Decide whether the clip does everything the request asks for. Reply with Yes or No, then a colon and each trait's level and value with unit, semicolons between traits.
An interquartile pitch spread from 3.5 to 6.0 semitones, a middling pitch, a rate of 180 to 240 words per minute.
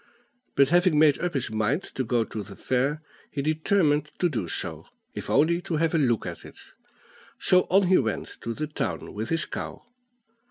Yes: wide, 5.4 semitones; medium, 150 Hz; average, 195 wpm